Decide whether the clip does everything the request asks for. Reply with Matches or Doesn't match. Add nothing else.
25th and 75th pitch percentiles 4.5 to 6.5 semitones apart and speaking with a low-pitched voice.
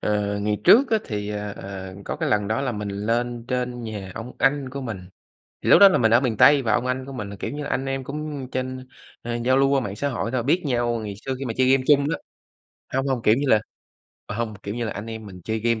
Doesn't match